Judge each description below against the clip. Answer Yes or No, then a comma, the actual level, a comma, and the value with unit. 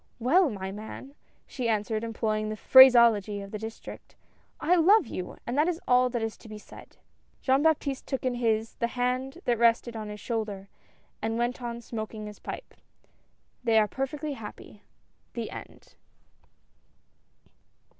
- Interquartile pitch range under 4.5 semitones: Yes, average, 3.4 semitones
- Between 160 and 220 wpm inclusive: Yes, average, 165 wpm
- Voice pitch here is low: No, high, 235 Hz